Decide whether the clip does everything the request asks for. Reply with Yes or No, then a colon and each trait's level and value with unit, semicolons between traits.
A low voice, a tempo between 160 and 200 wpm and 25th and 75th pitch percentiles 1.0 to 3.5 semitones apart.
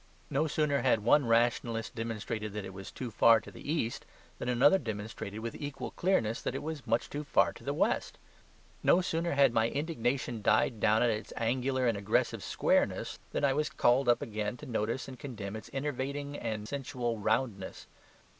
No: low, 120 Hz; average, 185 wpm; average, 4.2 semitones